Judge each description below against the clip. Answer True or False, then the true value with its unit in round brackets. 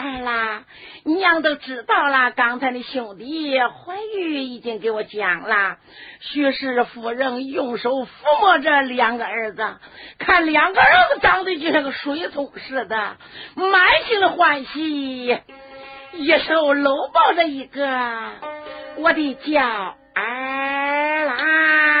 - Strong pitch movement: False (3.9 semitones)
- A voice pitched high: True (280 Hz)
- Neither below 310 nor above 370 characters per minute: False (175 characters per minute)